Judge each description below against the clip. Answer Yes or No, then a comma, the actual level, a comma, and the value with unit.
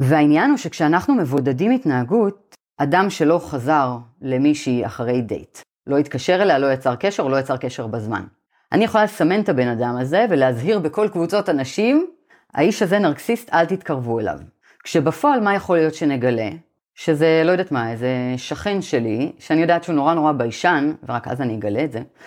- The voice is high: No, medium, 150 Hz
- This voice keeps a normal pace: No, fast, 165 wpm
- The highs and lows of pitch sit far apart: Yes, wide, 6.9 semitones